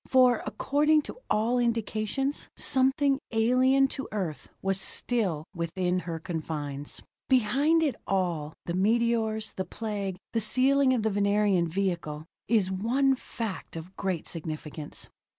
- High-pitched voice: Yes, high, 210 Hz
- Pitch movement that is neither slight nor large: No, wide, 6.1 semitones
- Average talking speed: No, slow, 130 wpm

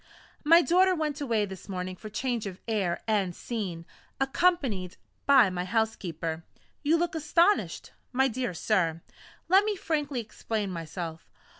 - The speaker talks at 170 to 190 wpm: No, average, 140 wpm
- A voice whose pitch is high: Yes, high, 220 Hz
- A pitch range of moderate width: No, wide, 8.4 semitones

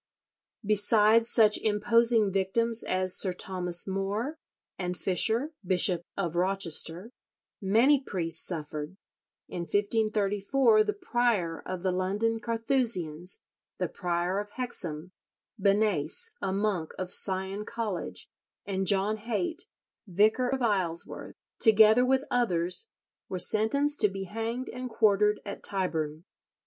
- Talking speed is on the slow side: Yes, slow, 115 wpm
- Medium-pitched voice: No, high, 205 Hz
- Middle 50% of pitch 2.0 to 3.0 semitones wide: No, average, 4.0 semitones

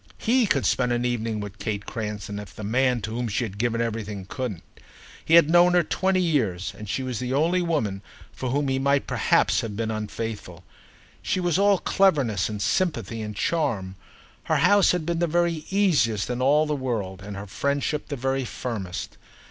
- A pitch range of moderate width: No, wide, 6.7 semitones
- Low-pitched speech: Yes, low, 125 Hz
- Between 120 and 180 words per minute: No, average, 195 wpm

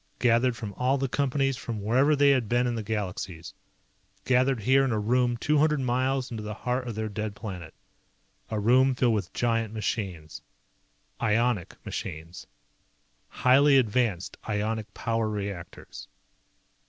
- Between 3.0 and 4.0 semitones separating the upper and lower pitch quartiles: Yes, average, 3.6 semitones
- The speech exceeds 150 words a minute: No, average, 145 wpm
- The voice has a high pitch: No, low, 115 Hz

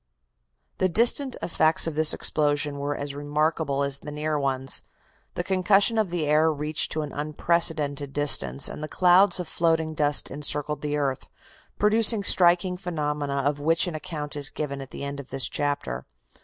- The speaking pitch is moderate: Yes, medium, 150 Hz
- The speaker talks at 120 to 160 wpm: No, average, 170 wpm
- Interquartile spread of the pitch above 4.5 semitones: No, average, 2.9 semitones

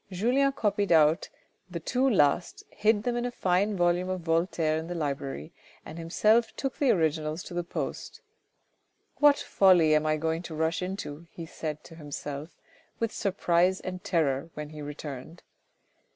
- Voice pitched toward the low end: No, medium, 170 Hz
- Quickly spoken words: No, average, 165 wpm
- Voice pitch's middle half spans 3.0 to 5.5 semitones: Yes, average, 4.0 semitones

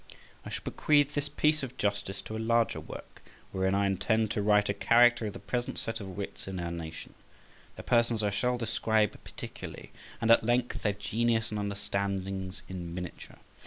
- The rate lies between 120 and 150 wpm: No, average, 185 wpm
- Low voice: Yes, low, 105 Hz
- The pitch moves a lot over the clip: No, average, 3.2 semitones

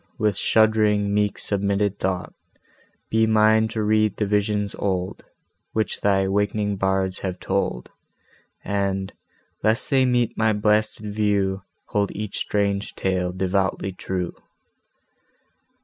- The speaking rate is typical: No, slow, 115 wpm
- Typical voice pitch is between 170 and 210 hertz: No, low, 100 Hz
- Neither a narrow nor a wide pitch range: No, narrow, 1.9 semitones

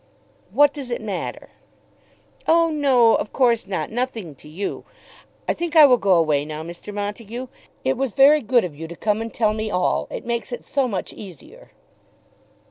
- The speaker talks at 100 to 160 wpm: No, average, 185 wpm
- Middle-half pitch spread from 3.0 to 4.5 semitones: No, average, 5.3 semitones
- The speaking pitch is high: Yes, high, 225 Hz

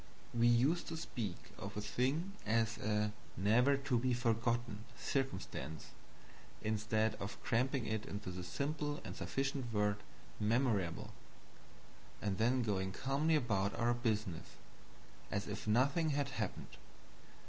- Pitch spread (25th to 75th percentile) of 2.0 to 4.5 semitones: Yes, average, 4.2 semitones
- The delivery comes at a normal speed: No, slow, 125 wpm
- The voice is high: No, low, 115 Hz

